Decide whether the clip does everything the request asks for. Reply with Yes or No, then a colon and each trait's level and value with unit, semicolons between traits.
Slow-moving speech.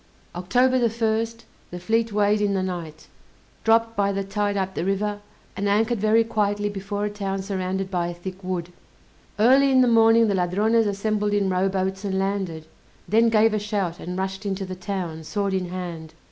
No: average, 190 wpm